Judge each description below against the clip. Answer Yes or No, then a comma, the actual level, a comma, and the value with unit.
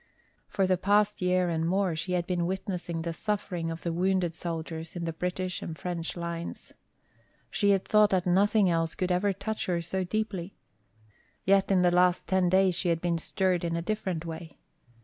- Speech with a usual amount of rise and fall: No, narrow, 2.2 semitones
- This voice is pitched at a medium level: Yes, medium, 180 Hz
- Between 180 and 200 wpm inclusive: Yes, average, 190 wpm